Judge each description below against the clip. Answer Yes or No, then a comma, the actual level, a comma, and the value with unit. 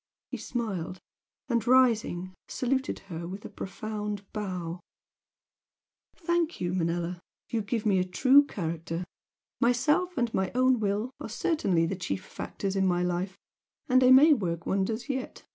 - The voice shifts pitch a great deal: Yes, wide, 5.9 semitones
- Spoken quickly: No, average, 145 wpm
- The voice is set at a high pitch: Yes, high, 205 Hz